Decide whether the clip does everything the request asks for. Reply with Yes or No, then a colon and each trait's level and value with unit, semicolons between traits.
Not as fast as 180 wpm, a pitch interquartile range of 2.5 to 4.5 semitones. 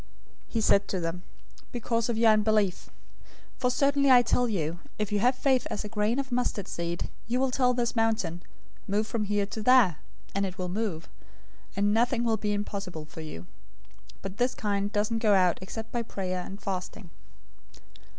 No: average, 190 wpm; average, 3.7 semitones